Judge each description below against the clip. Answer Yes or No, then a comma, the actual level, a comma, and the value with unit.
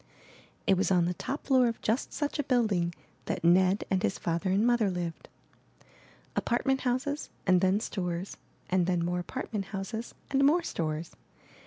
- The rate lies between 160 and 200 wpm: Yes, average, 165 wpm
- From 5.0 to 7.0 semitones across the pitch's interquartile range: Yes, wide, 5.5 semitones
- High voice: Yes, high, 195 Hz